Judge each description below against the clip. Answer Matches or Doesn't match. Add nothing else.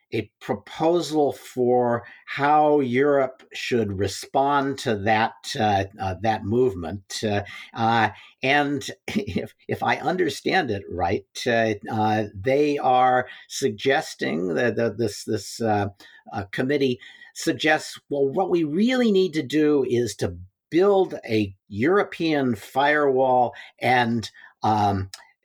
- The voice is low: Matches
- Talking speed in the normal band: Doesn't match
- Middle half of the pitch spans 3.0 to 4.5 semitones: Doesn't match